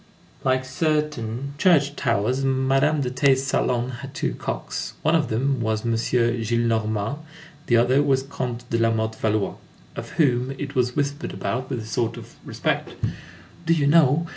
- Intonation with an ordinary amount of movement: Yes, average, 3.3 semitones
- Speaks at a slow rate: No, average, 160 wpm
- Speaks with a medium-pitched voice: No, low, 130 Hz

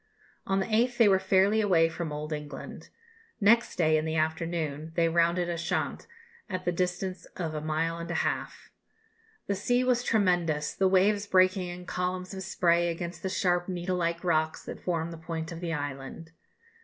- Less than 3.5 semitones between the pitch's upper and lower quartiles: Yes, narrow, 2.6 semitones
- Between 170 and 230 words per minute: Yes, average, 180 wpm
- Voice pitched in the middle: Yes, medium, 175 Hz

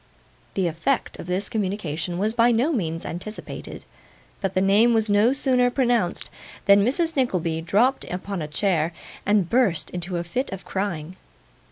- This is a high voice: Yes, high, 200 Hz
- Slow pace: No, average, 160 wpm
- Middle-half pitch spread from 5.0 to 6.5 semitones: Yes, average, 5.3 semitones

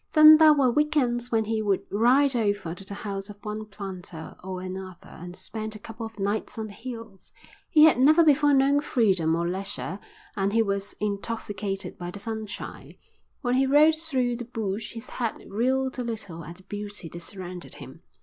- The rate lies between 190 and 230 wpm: Yes, average, 195 wpm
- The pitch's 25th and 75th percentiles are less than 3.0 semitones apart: No, average, 4.4 semitones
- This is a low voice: No, high, 215 Hz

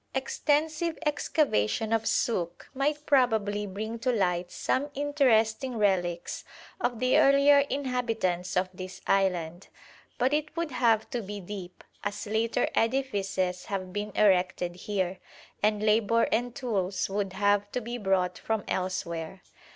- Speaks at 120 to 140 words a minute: Yes, slow, 135 wpm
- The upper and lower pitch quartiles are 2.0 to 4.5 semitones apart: No, average, 5.2 semitones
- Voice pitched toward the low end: No, high, 210 Hz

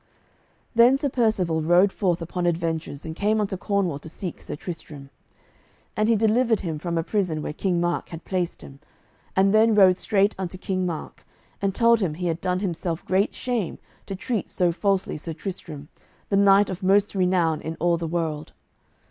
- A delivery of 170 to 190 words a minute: Yes, average, 185 wpm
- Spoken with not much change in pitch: No, average, 3.4 semitones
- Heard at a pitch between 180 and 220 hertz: Yes, medium, 185 Hz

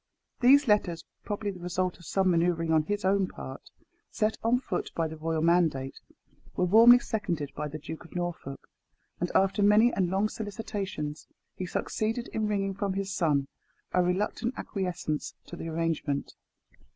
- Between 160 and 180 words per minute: Yes, average, 165 wpm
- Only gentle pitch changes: No, average, 4.0 semitones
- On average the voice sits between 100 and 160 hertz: No, medium, 185 Hz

